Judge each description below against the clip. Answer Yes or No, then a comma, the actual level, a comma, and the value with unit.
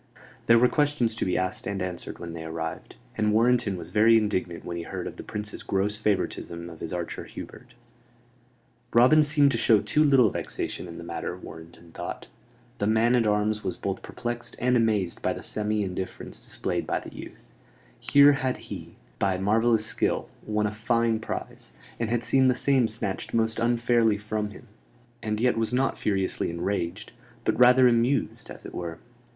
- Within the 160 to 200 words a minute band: Yes, average, 180 wpm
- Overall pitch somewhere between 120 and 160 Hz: No, low, 110 Hz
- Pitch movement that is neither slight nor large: Yes, average, 4.2 semitones